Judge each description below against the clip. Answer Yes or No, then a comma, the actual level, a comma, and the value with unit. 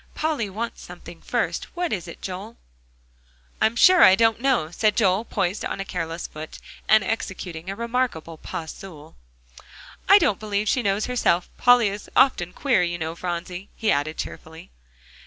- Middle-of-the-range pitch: No, high, 195 Hz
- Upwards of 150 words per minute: Yes, average, 165 wpm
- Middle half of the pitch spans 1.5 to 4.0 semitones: No, average, 5.3 semitones